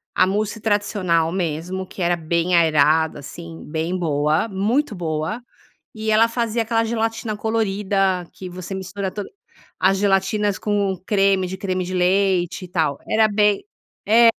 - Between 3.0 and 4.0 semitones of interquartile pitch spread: Yes, average, 3.3 semitones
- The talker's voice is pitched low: No, high, 190 Hz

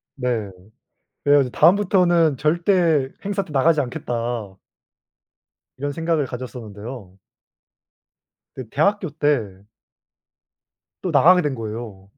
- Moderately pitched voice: Yes, medium, 145 Hz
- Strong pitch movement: Yes, wide, 5.8 semitones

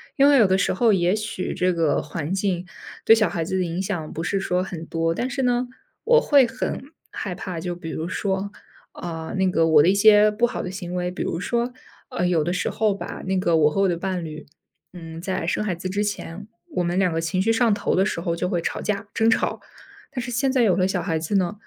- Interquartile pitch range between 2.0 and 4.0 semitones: Yes, average, 3.6 semitones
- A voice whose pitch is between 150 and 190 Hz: Yes, medium, 185 Hz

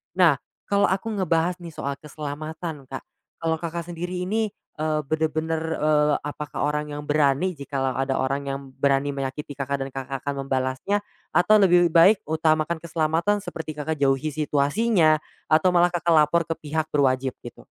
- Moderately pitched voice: Yes, medium, 155 Hz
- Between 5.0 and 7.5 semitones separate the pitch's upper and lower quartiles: No, average, 3.4 semitones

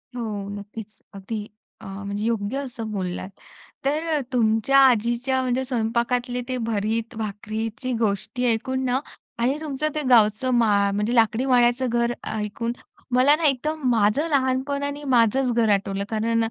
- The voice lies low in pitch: No, high, 235 Hz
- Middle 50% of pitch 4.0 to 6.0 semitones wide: No, average, 3.5 semitones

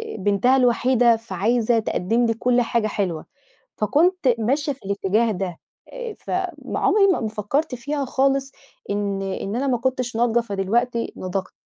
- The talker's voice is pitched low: No, high, 235 Hz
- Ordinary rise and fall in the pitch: Yes, average, 4.3 semitones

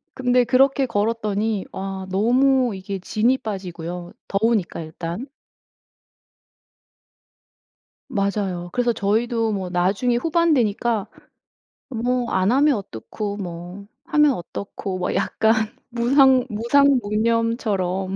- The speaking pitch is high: Yes, high, 215 Hz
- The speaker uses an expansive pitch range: No, average, 4.3 semitones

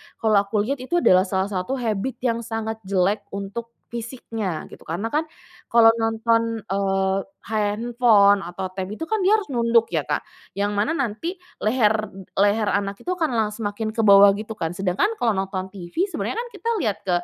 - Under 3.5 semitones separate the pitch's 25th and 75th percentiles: Yes, average, 2.9 semitones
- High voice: Yes, high, 215 Hz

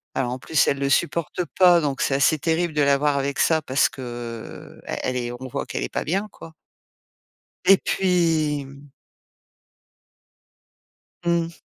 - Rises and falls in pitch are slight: No, average, 3.8 semitones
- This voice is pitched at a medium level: Yes, medium, 145 Hz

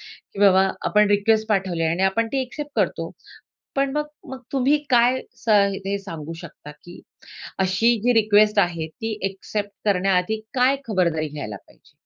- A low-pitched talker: No, high, 205 Hz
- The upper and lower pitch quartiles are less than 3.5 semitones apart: No, average, 4.1 semitones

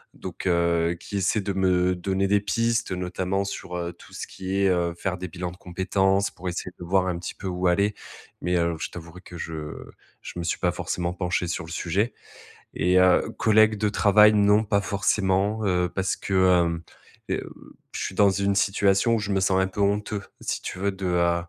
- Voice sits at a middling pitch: No, very low, 95 Hz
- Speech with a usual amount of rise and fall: No, narrow, 2.1 semitones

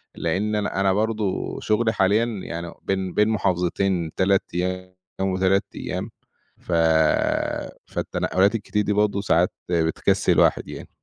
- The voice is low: Yes, very low, 95 Hz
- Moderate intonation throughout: No, narrow, 2.3 semitones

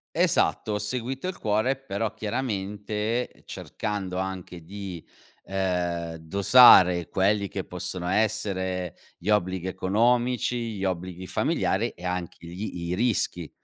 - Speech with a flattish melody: No, average, 3.1 semitones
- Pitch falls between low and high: No, very low, 95 Hz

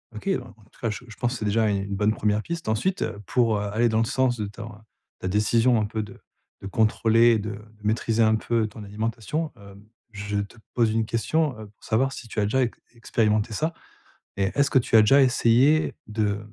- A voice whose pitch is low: Yes, low, 110 Hz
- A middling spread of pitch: No, narrow, 2.3 semitones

